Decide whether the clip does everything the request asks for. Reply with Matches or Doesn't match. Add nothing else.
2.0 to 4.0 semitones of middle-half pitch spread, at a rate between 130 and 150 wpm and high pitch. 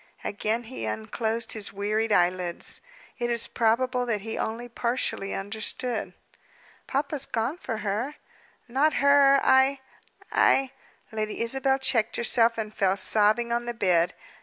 Matches